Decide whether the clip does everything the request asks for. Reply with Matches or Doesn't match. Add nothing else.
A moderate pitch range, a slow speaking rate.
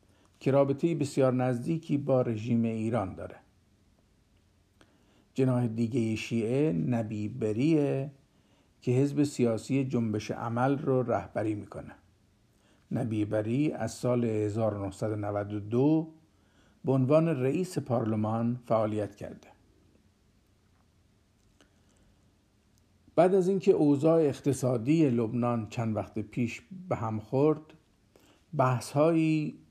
Matches